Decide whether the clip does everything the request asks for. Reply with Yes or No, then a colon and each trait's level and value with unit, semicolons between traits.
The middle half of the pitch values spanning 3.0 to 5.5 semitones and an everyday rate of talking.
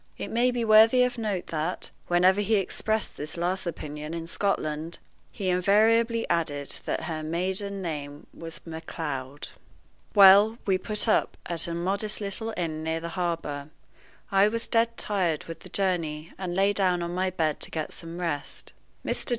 Yes: average, 4.0 semitones; average, 165 wpm